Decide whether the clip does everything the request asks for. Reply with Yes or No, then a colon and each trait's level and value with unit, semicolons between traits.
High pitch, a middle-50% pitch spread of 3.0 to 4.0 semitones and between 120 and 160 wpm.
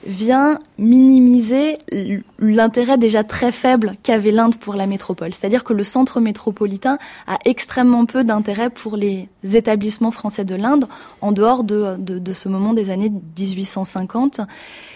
Yes: high, 220 Hz; average, 3.5 semitones; slow, 145 wpm